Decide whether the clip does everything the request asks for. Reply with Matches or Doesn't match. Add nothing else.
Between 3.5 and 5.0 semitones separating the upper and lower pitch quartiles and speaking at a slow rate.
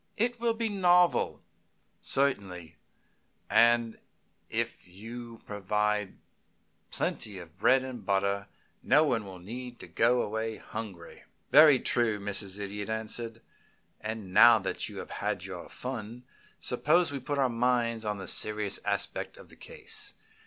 Matches